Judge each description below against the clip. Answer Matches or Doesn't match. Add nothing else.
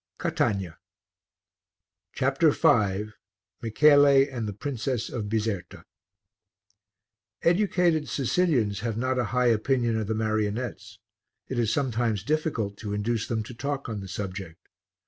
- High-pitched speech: Doesn't match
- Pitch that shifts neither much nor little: Matches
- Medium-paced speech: Doesn't match